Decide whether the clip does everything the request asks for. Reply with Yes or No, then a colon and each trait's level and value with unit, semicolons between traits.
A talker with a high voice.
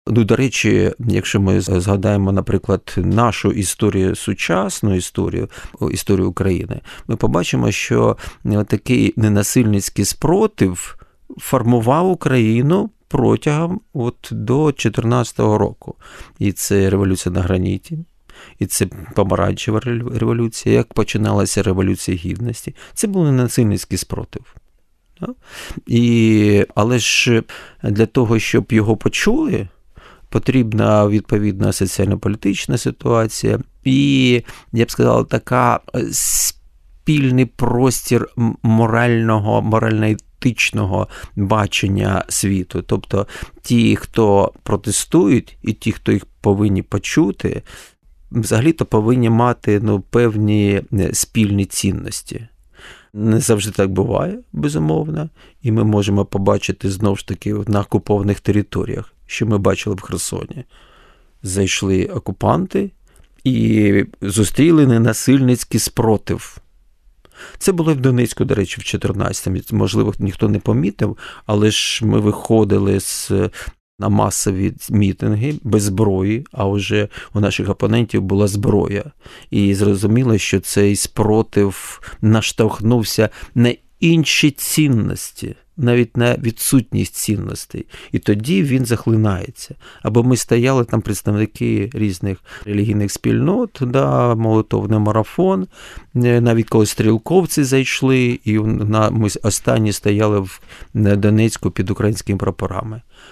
No: low, 110 Hz